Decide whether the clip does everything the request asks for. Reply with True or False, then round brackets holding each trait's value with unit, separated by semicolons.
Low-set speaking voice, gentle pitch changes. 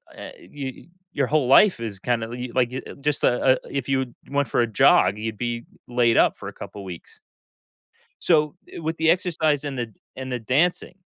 False (130 Hz; 3.8 semitones)